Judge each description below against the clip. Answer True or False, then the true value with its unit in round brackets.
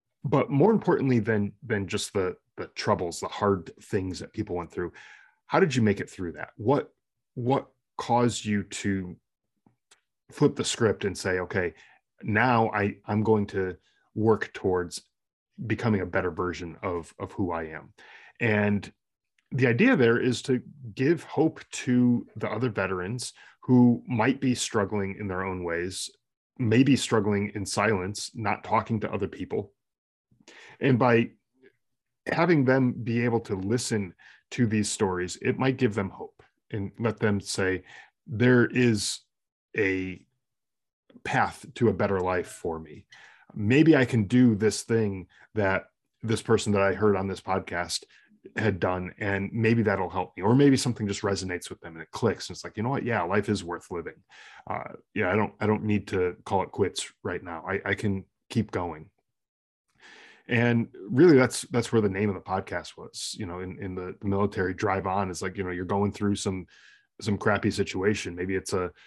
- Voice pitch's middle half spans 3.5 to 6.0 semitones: True (3.8 semitones)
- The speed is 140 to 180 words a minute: True (175 wpm)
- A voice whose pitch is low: True (105 Hz)